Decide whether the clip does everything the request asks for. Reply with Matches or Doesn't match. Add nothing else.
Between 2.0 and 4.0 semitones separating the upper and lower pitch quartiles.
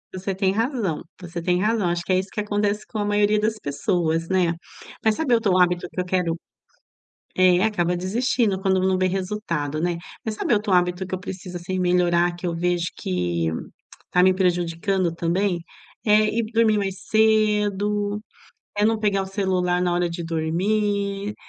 Matches